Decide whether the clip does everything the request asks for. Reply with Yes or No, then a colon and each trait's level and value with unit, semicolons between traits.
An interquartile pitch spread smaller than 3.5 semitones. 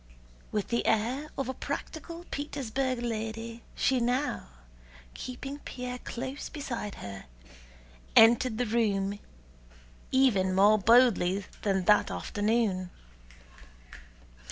No: average, 3.8 semitones